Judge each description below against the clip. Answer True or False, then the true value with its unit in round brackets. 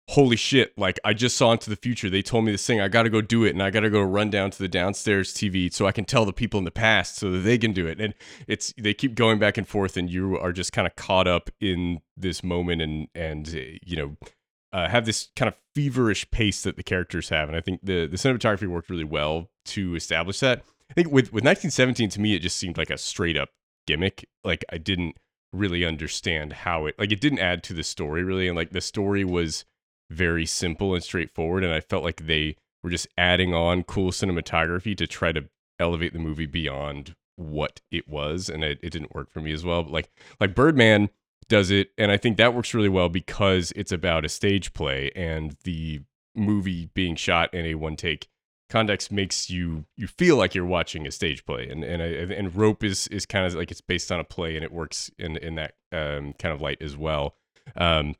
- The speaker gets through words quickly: True (235 wpm)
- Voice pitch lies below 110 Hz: True (90 Hz)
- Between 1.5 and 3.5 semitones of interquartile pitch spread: False (4.1 semitones)